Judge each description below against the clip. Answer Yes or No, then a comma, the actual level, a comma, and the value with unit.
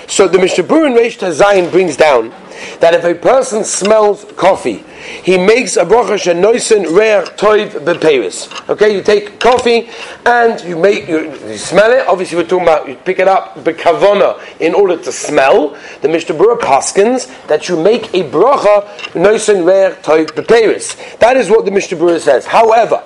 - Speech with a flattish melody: No, average, 4.4 semitones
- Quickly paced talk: No, average, 170 wpm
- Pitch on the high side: Yes, high, 205 Hz